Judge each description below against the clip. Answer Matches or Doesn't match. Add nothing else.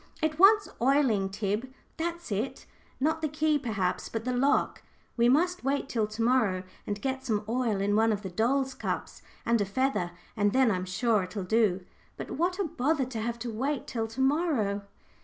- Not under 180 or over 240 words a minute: Matches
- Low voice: Doesn't match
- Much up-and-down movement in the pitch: Doesn't match